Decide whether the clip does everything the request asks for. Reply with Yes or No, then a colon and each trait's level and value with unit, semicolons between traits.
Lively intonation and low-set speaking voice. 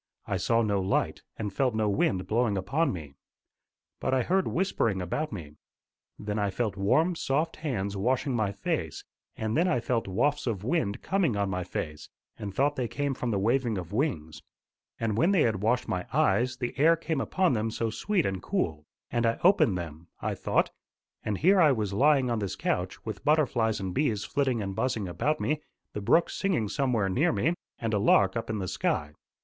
Yes: wide, 6.3 semitones; low, 115 Hz